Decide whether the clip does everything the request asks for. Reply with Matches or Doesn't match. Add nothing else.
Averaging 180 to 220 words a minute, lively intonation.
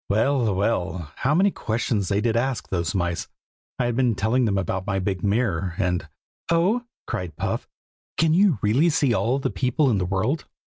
Matches